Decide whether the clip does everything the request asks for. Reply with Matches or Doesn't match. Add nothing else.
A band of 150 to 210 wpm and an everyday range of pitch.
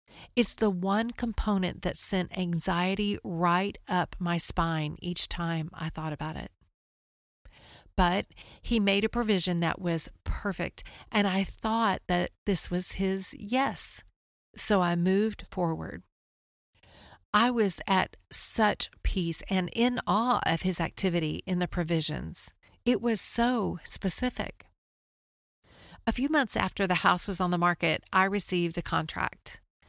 Doesn't match